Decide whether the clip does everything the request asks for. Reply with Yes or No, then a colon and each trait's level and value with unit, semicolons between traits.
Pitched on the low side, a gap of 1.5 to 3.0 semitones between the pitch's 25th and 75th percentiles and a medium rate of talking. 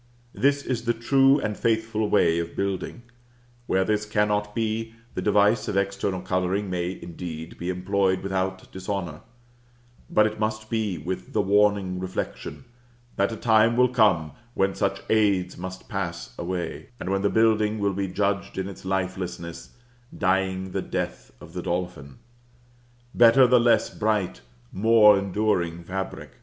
Yes: low, 100 Hz; average, 2.7 semitones; average, 150 wpm